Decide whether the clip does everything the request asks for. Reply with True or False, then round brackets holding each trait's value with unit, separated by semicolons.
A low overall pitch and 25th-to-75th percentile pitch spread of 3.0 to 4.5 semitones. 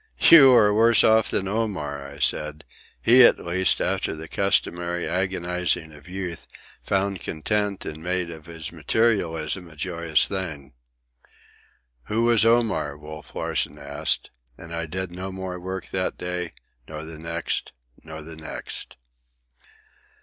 True (90 Hz; 3.6 semitones)